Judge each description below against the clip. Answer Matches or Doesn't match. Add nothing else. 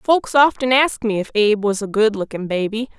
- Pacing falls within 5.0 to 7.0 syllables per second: Matches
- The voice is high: Matches